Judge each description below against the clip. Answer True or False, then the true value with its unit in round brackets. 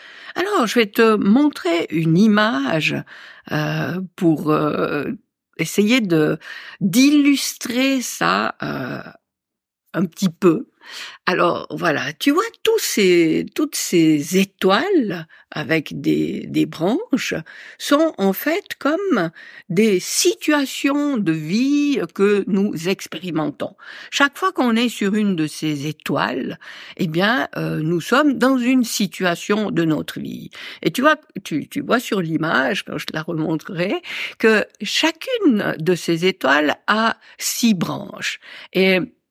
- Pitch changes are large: True (8.7 semitones)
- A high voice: True (210 Hz)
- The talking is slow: True (125 wpm)